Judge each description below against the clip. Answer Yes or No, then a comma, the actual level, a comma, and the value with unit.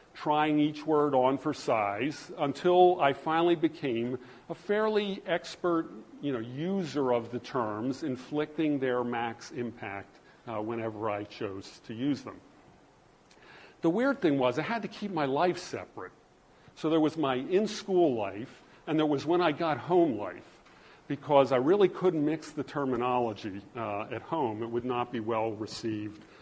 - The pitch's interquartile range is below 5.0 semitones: No, wide, 5.5 semitones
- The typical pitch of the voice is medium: Yes, medium, 145 Hz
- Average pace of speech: Yes, average, 165 wpm